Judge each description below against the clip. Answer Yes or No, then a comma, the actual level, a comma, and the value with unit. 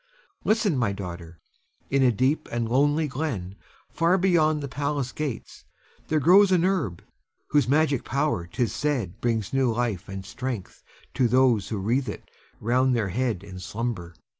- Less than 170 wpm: Yes, average, 160 wpm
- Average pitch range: No, wide, 6.1 semitones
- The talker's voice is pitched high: No, low, 125 Hz